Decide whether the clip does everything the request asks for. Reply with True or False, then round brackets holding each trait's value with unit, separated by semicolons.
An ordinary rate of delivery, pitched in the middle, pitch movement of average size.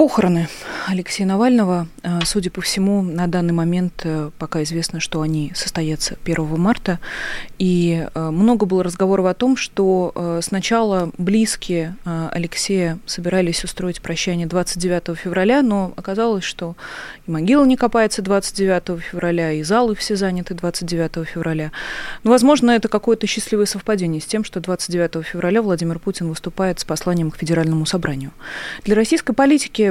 True (135 wpm; 180 Hz; 3.6 semitones)